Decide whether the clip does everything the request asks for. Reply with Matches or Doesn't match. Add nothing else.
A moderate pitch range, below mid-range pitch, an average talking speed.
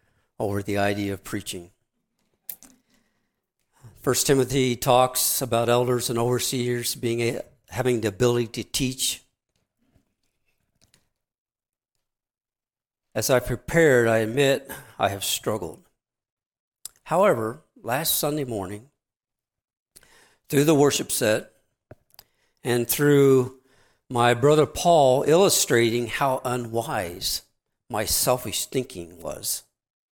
Doesn't match